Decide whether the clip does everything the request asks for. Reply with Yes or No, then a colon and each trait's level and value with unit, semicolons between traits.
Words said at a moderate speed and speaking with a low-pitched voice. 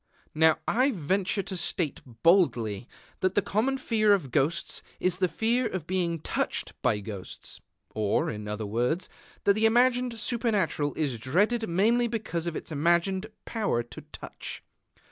No: average, 150 wpm; medium, 180 Hz